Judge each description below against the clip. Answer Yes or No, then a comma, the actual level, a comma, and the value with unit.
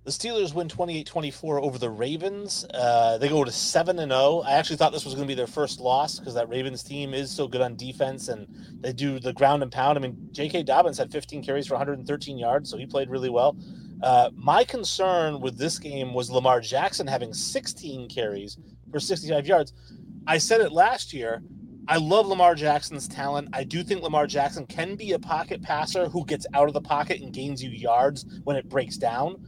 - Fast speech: Yes, fast, 215 wpm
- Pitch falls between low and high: Yes, medium, 145 Hz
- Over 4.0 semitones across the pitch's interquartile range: Yes, average, 4.4 semitones